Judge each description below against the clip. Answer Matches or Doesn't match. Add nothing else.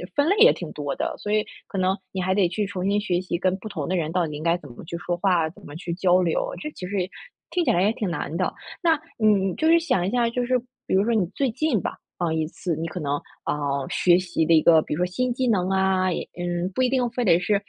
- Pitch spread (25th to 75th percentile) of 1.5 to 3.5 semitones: Doesn't match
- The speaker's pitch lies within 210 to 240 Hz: Doesn't match